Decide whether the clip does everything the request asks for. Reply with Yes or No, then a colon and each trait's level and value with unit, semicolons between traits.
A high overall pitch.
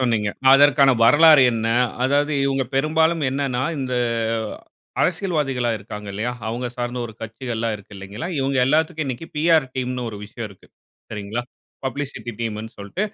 No: low, 130 Hz